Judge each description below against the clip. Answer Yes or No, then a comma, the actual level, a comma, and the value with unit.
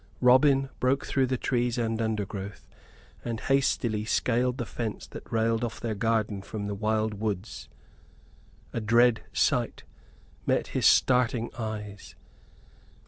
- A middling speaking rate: No, slow, 130 wpm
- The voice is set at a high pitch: No, low, 115 Hz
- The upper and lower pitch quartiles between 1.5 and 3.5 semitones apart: Yes, narrow, 2.4 semitones